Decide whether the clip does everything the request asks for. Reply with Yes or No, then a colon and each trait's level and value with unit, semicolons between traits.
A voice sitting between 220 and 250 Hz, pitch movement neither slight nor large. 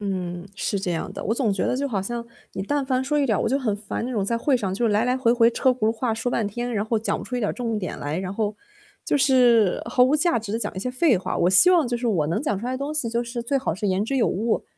Yes: high, 230 Hz; average, 3.9 semitones